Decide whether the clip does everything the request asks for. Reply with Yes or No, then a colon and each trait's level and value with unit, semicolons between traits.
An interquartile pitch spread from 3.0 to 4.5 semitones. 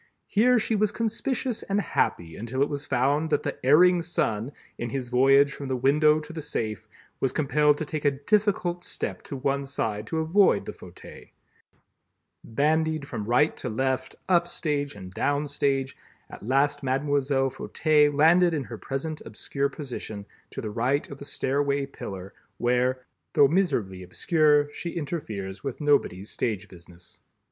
Yes: average, 3.8 semitones